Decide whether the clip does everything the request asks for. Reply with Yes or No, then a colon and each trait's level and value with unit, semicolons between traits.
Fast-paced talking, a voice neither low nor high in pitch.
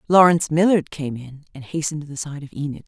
Yes: fast, 230 wpm; medium, 150 Hz